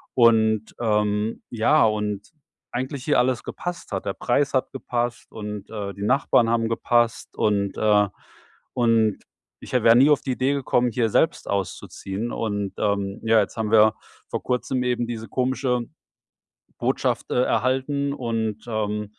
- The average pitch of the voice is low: Yes, low, 115 Hz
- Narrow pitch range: No, average, 3.0 semitones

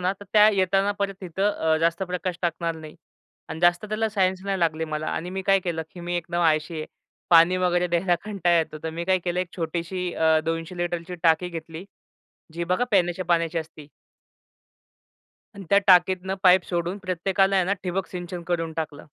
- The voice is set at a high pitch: No, medium, 175 Hz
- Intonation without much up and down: Yes, narrow, 2.1 semitones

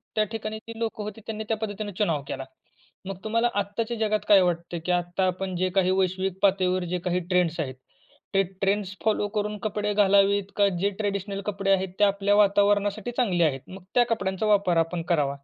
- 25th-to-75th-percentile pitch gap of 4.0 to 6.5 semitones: No, narrow, 2.4 semitones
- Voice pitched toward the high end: Yes, high, 200 Hz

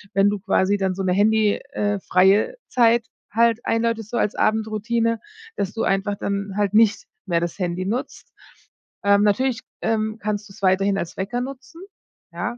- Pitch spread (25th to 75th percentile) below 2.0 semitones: No, narrow, 2.6 semitones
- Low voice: No, high, 210 Hz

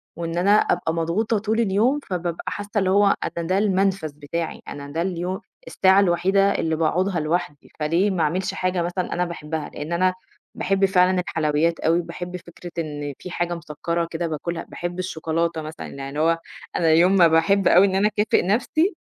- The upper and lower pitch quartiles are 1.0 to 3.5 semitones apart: Yes, average, 2.8 semitones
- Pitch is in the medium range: Yes, medium, 175 Hz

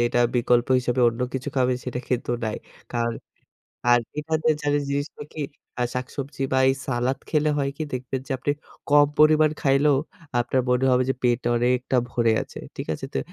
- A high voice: No, low, 130 Hz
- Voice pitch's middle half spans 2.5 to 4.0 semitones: Yes, average, 2.8 semitones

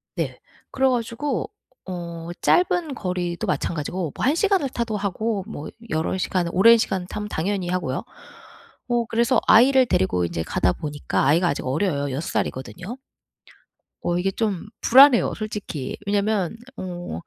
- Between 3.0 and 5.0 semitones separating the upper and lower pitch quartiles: No, wide, 5.4 semitones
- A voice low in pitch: No, high, 190 Hz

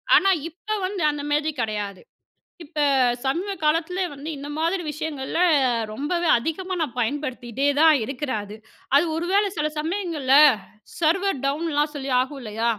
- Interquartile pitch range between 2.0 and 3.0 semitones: No, average, 3.9 semitones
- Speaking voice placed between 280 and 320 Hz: Yes, very high, 300 Hz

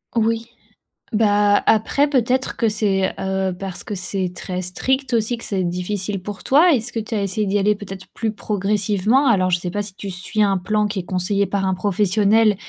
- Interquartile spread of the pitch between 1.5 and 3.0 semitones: Yes, narrow, 2.6 semitones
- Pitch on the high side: Yes, high, 205 Hz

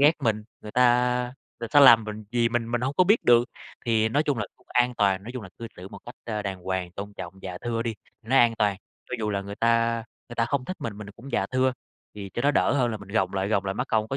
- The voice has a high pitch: No, low, 115 Hz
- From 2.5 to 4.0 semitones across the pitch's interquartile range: Yes, average, 3.2 semitones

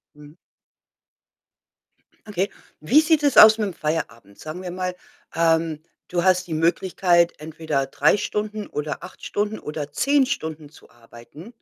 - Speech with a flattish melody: No, average, 5.1 semitones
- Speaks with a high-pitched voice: No, medium, 170 Hz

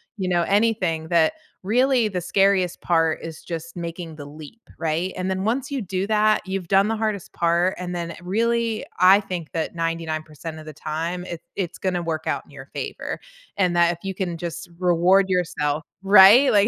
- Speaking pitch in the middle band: Yes, medium, 180 Hz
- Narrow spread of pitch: No, average, 3.0 semitones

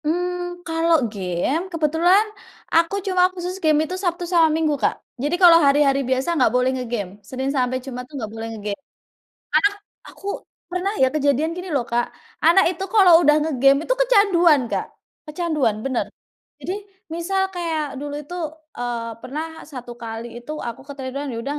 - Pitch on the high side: Yes, very high, 300 Hz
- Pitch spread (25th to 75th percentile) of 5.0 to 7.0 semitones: Yes, average, 5.3 semitones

